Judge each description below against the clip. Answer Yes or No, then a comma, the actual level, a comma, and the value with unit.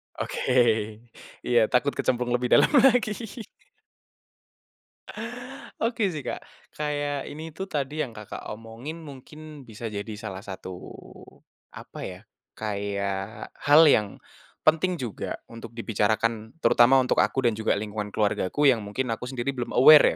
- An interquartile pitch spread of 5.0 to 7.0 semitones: Yes, average, 5.3 semitones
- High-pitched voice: No, low, 120 Hz